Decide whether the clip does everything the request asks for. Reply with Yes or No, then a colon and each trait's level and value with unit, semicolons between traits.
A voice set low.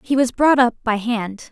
No: high, 240 Hz